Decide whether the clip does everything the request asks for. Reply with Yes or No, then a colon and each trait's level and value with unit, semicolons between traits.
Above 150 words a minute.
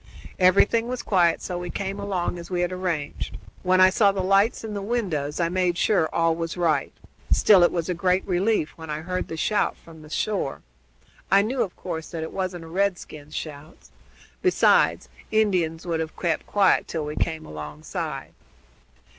Yes: average, 185 wpm